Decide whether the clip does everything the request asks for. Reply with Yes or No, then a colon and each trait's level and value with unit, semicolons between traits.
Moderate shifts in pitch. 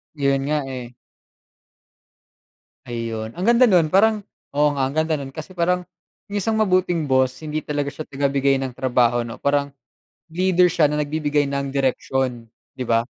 Yes: average, 4.0 semitones